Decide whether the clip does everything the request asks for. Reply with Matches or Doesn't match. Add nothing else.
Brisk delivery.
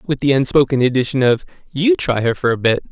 Matches